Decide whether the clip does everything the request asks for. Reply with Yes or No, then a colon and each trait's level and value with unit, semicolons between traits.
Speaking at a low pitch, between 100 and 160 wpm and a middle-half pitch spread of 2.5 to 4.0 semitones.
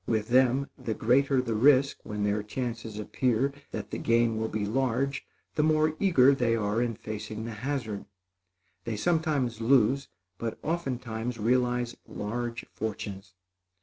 Yes: low, 120 Hz; average, 145 wpm; average, 3.5 semitones